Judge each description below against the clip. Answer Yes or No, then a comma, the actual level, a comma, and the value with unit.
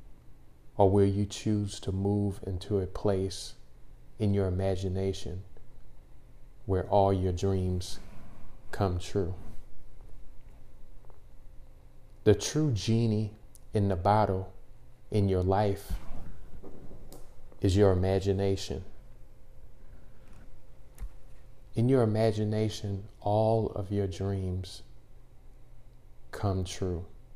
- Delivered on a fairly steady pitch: Yes, narrow, 2.2 semitones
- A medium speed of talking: No, slow, 85 wpm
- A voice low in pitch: Yes, low, 100 Hz